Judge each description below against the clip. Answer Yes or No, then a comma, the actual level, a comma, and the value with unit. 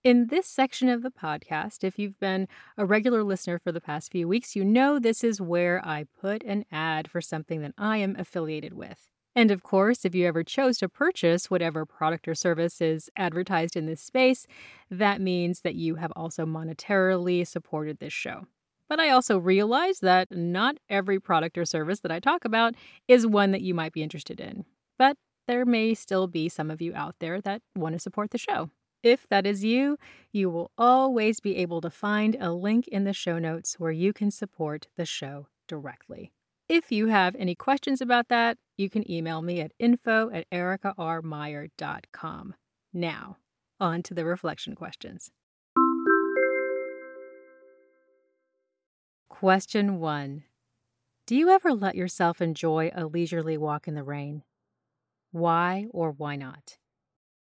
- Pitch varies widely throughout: No, average, 4.7 semitones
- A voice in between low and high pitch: Yes, medium, 180 Hz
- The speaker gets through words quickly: No, average, 170 wpm